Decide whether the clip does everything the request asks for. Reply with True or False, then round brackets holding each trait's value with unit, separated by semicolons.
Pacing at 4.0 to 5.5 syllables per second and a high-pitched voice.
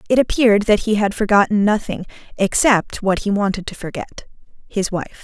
True (5.4 syllables/s; 205 Hz)